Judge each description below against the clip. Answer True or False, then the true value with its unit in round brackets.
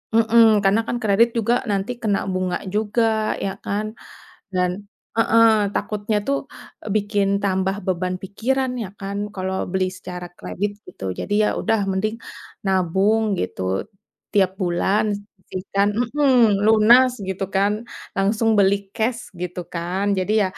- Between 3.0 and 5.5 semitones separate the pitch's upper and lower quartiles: False (2.5 semitones)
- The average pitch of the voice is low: False (205 Hz)